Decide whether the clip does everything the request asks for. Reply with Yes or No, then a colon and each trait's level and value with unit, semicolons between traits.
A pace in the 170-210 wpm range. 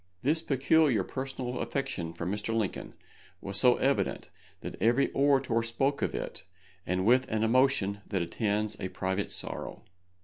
No: average, 145 wpm